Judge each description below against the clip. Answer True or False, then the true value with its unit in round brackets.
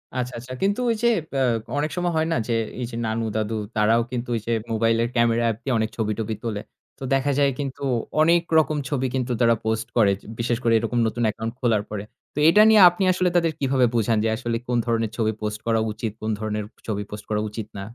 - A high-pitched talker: False (115 Hz)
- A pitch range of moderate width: True (3.4 semitones)